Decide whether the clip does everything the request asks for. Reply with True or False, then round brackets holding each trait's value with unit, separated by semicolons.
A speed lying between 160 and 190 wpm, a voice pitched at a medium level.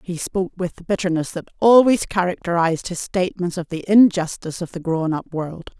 True (185 wpm; 180 Hz)